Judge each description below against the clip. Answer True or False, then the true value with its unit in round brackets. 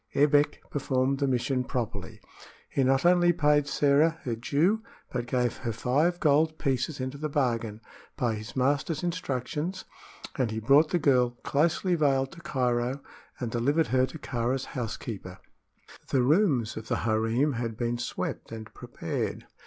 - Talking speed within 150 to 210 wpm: True (155 wpm)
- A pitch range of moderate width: True (3.7 semitones)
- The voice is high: False (135 Hz)